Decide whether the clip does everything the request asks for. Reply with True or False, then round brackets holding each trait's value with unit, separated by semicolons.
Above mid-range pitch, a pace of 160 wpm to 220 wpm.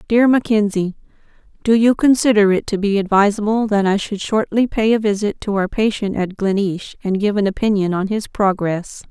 True (205 Hz; 185 wpm)